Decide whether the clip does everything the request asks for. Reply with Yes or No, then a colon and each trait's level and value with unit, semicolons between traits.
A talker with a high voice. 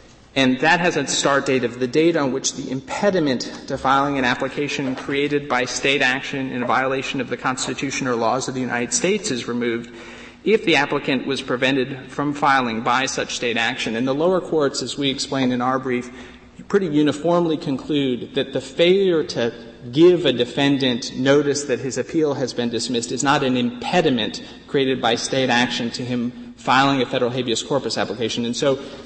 No: low, 135 Hz